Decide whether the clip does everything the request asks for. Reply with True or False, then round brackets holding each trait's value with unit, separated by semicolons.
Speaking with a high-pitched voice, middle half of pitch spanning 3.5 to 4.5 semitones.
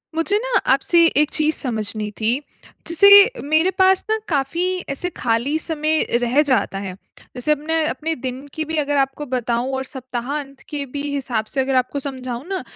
True (280 Hz; 3.8 semitones)